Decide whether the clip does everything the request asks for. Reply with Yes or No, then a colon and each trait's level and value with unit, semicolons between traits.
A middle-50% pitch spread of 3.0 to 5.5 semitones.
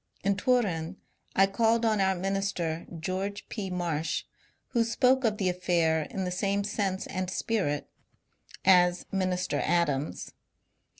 No: narrow, 2.5 semitones